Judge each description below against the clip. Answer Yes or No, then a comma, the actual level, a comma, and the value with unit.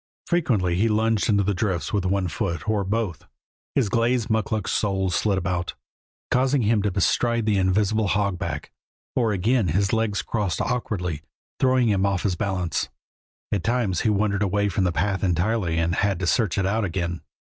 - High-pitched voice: No, low, 100 Hz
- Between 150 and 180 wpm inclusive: Yes, average, 175 wpm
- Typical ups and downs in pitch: Yes, average, 3.2 semitones